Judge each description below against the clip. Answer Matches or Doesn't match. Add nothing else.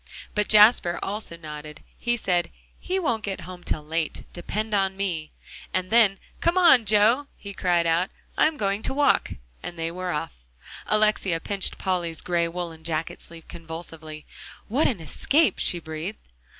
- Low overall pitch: Doesn't match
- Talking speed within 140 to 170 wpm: Matches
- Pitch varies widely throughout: Doesn't match